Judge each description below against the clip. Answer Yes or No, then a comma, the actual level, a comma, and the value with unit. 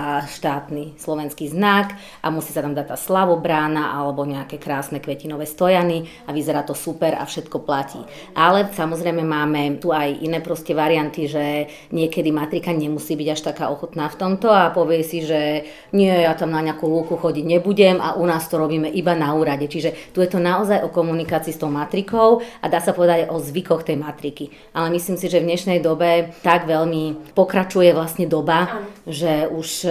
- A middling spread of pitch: No, narrow, 2.3 semitones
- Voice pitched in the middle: Yes, medium, 160 Hz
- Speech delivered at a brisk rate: Yes, fast, 190 wpm